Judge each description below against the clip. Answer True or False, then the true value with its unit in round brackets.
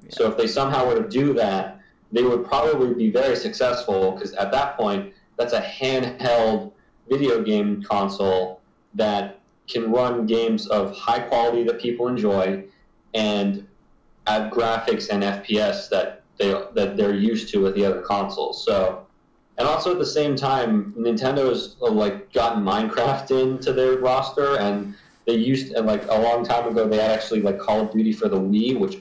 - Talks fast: False (170 wpm)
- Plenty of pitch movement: False (3.9 semitones)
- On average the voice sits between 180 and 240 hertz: False (115 Hz)